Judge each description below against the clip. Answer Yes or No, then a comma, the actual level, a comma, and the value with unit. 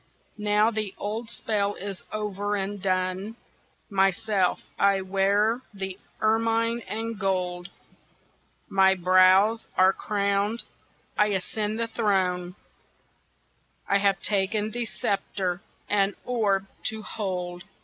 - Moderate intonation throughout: No, narrow, 2.1 semitones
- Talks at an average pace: No, slow, 110 wpm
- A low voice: No, high, 200 Hz